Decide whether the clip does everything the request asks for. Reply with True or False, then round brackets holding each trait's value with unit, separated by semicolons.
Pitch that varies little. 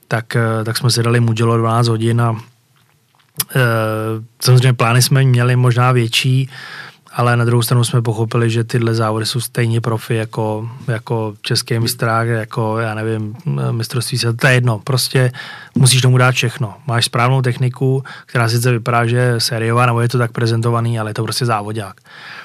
True (1.7 semitones)